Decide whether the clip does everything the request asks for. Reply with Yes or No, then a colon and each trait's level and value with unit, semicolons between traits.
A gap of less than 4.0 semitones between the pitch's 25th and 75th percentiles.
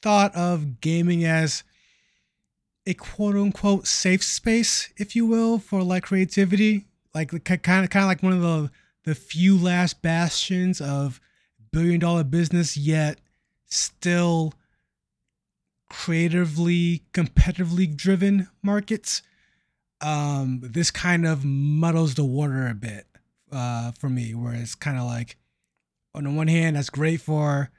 No: average, 4.4 semitones